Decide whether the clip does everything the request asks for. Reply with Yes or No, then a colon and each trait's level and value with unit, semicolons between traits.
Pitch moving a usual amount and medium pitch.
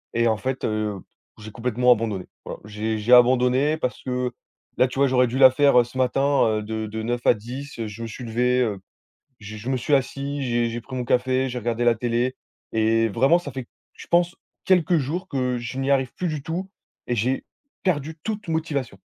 No: average, 3.0 semitones; low, 125 Hz